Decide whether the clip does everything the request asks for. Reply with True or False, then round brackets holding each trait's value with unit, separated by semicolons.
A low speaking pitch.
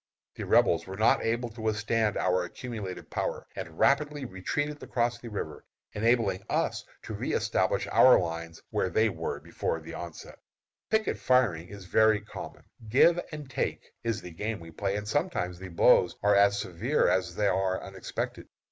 True (105 Hz)